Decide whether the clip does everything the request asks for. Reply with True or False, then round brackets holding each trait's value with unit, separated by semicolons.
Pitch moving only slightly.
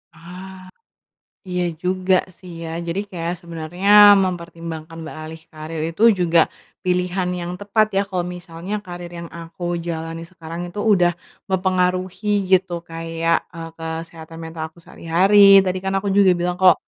True (2.1 semitones)